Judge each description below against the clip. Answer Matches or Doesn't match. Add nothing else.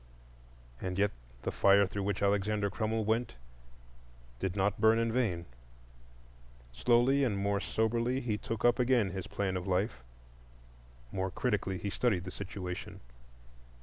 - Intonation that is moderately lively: Matches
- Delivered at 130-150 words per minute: Matches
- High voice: Doesn't match